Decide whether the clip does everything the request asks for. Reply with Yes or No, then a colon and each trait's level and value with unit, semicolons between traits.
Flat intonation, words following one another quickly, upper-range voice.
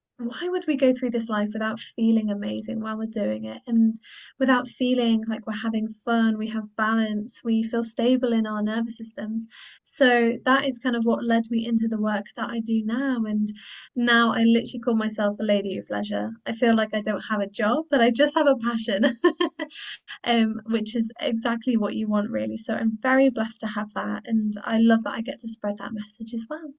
Yes: narrow, 2.2 semitones; fast, 215 wpm; high, 225 Hz